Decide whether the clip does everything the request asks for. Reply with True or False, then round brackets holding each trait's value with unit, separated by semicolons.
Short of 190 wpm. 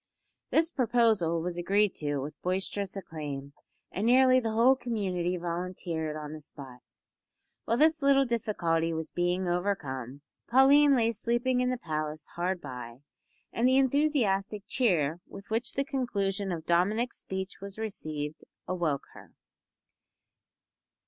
True (135 wpm)